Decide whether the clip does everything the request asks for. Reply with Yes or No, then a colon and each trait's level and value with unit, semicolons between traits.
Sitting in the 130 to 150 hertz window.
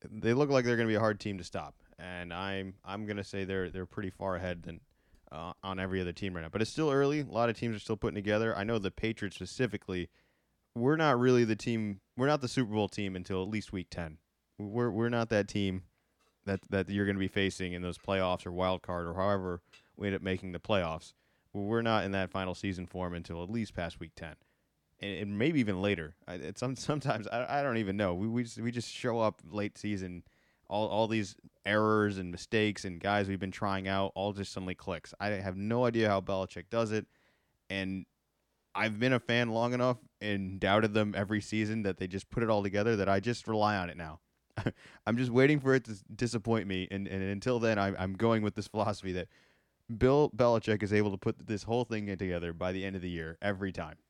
No: low, 100 Hz